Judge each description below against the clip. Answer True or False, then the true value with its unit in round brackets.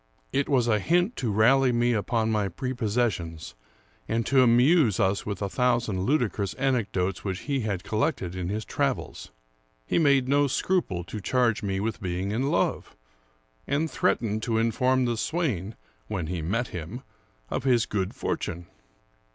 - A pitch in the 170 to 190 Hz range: False (115 Hz)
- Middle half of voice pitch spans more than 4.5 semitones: True (4.9 semitones)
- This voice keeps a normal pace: True (160 wpm)